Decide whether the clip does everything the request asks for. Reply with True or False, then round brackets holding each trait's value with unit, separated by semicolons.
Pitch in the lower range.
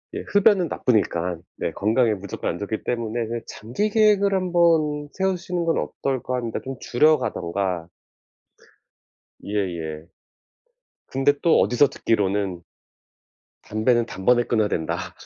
True (120 Hz)